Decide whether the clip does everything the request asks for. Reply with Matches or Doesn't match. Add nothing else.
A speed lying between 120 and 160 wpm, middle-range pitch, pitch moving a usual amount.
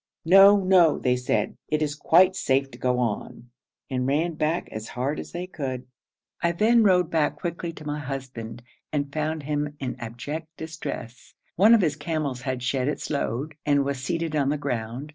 Doesn't match